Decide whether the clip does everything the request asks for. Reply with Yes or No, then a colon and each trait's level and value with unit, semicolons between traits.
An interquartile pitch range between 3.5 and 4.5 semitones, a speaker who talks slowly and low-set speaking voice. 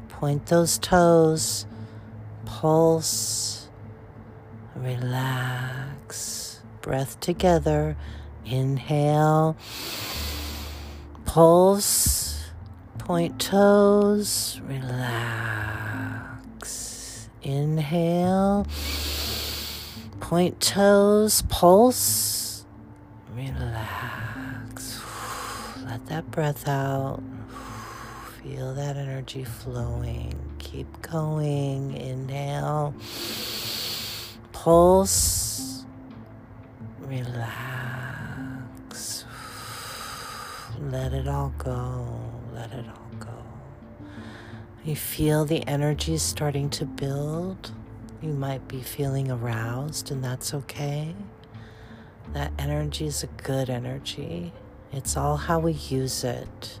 Yes: average, 4.2 semitones; slow, 70 wpm; low, 120 Hz